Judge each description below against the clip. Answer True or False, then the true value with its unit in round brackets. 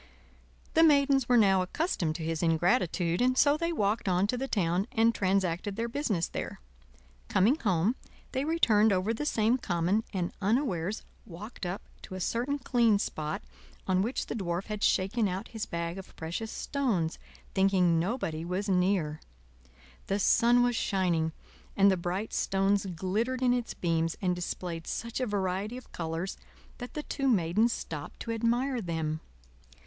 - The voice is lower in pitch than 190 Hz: False (195 Hz)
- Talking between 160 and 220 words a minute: True (165 wpm)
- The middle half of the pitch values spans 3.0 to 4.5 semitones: False (5.1 semitones)